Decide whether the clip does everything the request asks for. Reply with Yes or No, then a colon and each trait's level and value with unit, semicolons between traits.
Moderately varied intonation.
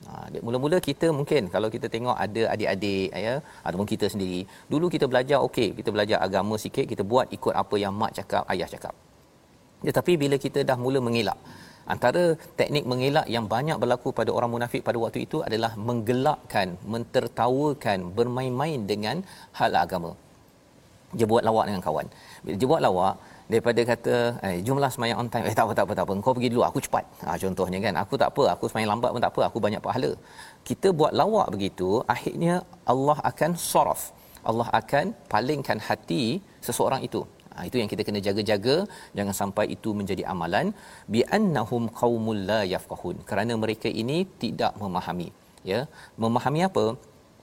Yes: average, 4.2 semitones